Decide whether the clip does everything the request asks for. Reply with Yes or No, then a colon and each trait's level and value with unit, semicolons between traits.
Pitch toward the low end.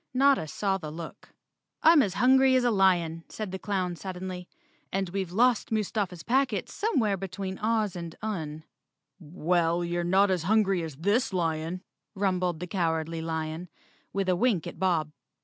No: medium, 185 Hz